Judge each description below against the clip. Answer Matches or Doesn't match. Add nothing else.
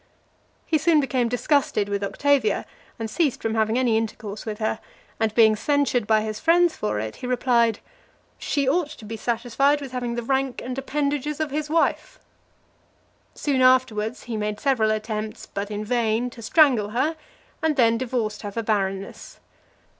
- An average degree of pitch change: Matches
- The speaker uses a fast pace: Doesn't match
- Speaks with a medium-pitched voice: Doesn't match